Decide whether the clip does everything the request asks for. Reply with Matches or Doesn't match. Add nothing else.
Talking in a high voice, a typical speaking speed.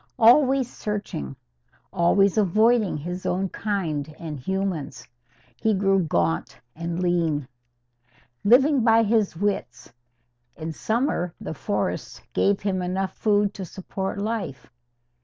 Doesn't match